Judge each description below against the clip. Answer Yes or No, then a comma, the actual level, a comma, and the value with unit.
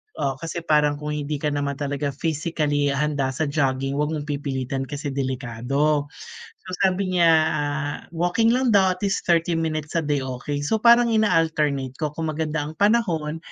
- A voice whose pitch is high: No, medium, 150 Hz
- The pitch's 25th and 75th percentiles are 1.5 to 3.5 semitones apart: Yes, narrow, 2.5 semitones